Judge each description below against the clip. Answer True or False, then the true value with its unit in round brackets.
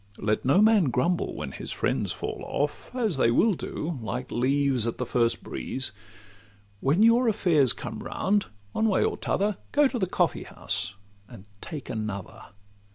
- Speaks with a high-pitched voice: False (145 Hz)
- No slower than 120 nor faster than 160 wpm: False (170 wpm)